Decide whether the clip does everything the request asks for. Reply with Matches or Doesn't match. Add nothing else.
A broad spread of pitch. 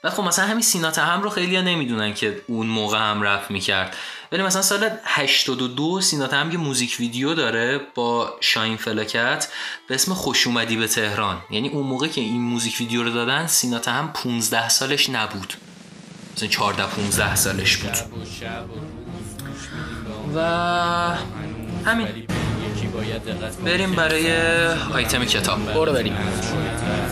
Matches